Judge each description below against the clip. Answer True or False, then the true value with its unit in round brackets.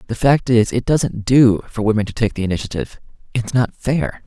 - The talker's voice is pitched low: True (115 Hz)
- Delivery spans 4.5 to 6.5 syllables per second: True (5.4 syllables/s)